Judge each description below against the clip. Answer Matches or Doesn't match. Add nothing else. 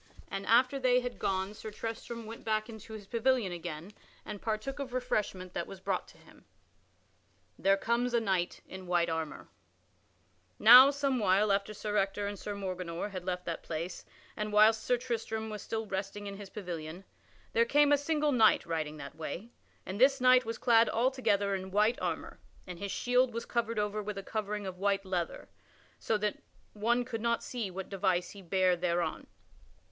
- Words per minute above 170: Matches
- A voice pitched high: Matches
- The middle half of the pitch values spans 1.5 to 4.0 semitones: Matches